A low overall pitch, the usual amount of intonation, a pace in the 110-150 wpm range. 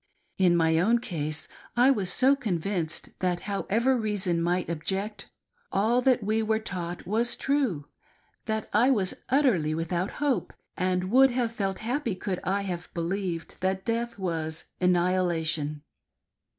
No: high, 190 Hz; average, 4.9 semitones; average, 145 wpm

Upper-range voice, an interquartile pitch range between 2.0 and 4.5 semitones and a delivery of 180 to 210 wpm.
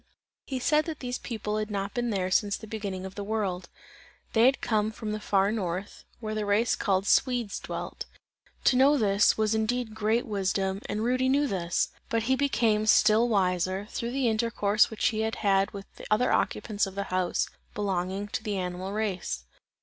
Yes: high, 210 Hz; average, 2.9 semitones; average, 190 wpm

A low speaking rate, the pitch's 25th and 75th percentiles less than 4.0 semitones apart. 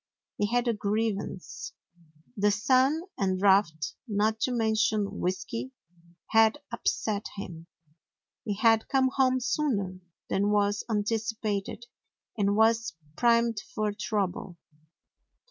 Yes: slow, 110 wpm; narrow, 2.4 semitones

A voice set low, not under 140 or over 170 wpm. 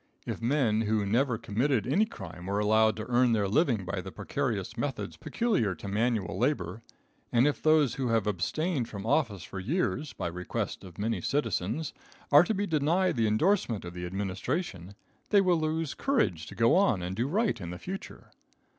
No: low, 115 Hz; average, 185 wpm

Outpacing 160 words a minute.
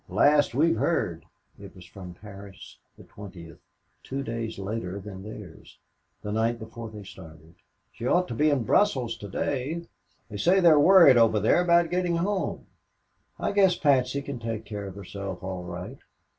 Yes: average, 170 wpm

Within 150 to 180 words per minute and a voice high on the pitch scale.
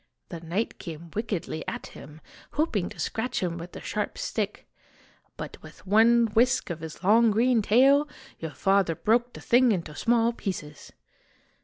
Yes: average, 160 wpm; high, 210 Hz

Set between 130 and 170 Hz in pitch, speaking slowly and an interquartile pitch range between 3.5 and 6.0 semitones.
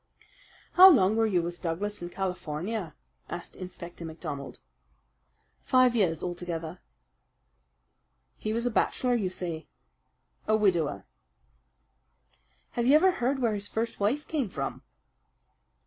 No: high, 195 Hz; slow, 120 wpm; wide, 5.4 semitones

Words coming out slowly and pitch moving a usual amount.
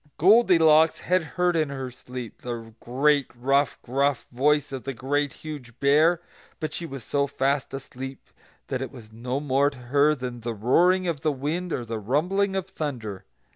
No: average, 175 wpm; average, 3.7 semitones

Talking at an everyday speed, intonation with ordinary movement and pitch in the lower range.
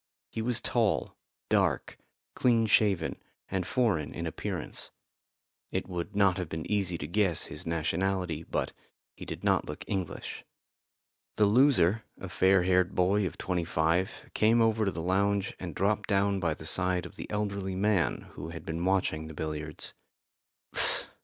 Yes: average, 160 wpm; average, 3.5 semitones; very low, 95 Hz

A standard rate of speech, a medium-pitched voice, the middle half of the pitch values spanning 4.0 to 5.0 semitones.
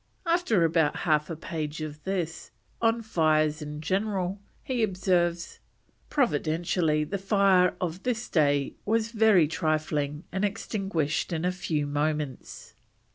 No: slow, 130 wpm; medium, 170 Hz; average, 4.3 semitones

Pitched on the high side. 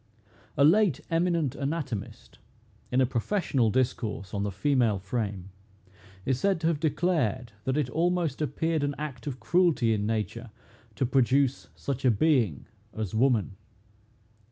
No: low, 130 Hz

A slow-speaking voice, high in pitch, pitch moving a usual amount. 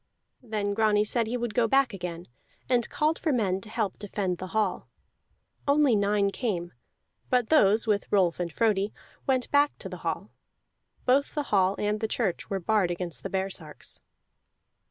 No: average, 170 wpm; high, 210 Hz; average, 4.0 semitones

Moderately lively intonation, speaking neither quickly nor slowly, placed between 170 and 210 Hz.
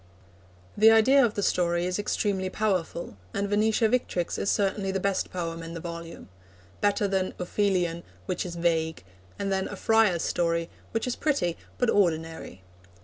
Yes: average, 3.4 semitones; average, 160 wpm; high, 190 Hz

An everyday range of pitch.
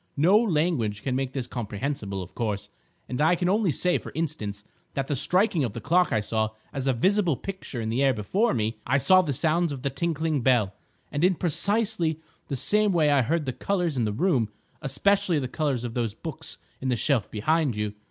No: wide, 6.5 semitones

